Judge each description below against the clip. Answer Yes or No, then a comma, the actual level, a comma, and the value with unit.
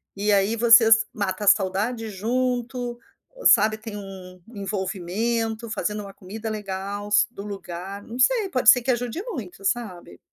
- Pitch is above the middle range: Yes, high, 210 Hz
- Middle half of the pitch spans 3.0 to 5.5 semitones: Yes, average, 3.3 semitones